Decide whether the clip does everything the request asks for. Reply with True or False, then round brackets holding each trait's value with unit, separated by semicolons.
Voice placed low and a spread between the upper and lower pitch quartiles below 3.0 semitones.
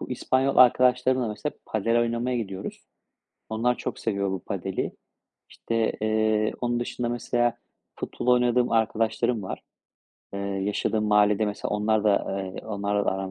True (110 Hz; 2.6 semitones)